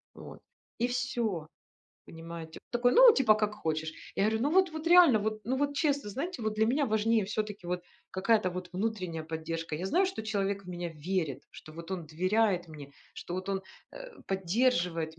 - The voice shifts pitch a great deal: Yes, wide, 5.8 semitones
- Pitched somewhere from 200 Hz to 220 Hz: Yes, high, 205 Hz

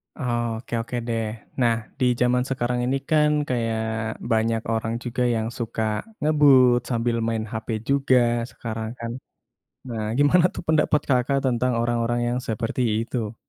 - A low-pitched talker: Yes, low, 120 Hz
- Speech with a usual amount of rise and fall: No, narrow, 2.2 semitones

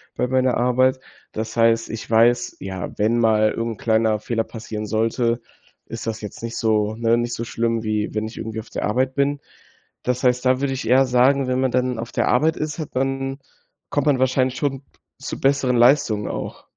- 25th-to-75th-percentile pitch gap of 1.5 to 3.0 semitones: Yes, narrow, 2.6 semitones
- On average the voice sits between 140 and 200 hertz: No, low, 120 Hz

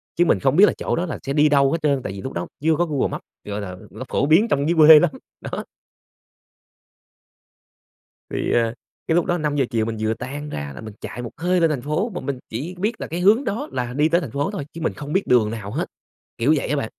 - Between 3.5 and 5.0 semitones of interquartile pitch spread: No, wide, 5.5 semitones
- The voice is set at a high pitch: No, medium, 145 Hz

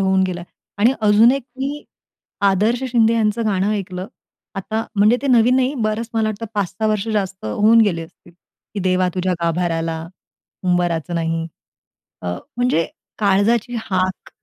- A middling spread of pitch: Yes, average, 3.7 semitones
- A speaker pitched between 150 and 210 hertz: Yes, high, 205 Hz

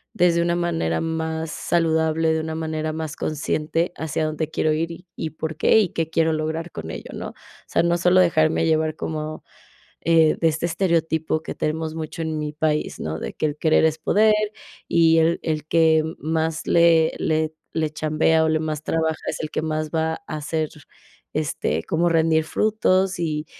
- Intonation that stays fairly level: Yes, narrow, 1.0 semitones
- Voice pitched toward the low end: No, medium, 160 Hz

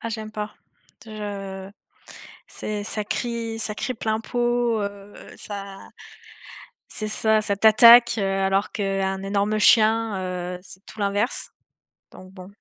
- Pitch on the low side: No, high, 210 Hz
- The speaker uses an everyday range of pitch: No, narrow, 2.2 semitones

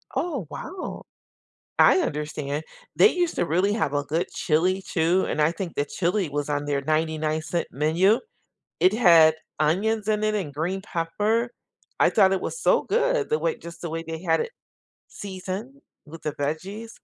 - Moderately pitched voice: Yes, medium, 175 Hz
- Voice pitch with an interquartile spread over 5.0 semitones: Yes, wide, 5.4 semitones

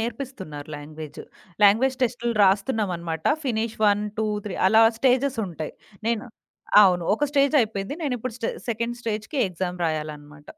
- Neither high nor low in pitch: No, high, 215 Hz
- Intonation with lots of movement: Yes, wide, 5.7 semitones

